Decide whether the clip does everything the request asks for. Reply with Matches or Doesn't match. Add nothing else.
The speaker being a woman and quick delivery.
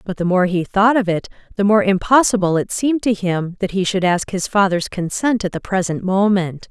Matches